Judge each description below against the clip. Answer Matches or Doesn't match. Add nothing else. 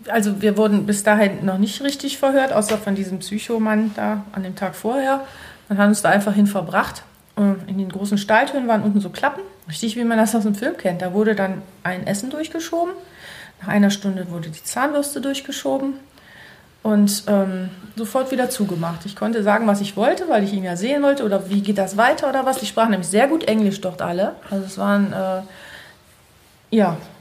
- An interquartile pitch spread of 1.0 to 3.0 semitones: Doesn't match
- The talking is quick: Matches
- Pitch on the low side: Doesn't match